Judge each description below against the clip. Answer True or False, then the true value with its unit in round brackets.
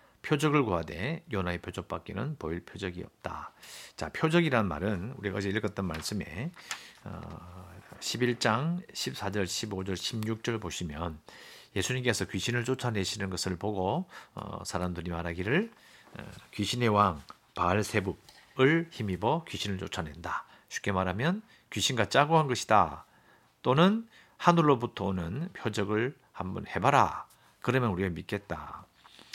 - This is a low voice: True (105 Hz)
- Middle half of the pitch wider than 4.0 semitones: True (5.3 semitones)